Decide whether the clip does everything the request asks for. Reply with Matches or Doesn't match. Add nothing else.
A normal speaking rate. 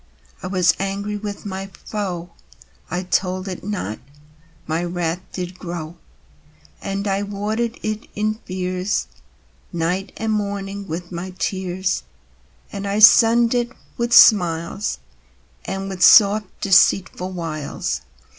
Doesn't match